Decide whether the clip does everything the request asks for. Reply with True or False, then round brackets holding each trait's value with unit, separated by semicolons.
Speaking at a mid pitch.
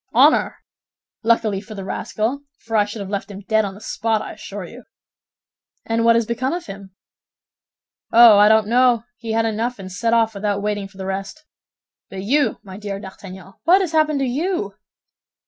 False (220 Hz)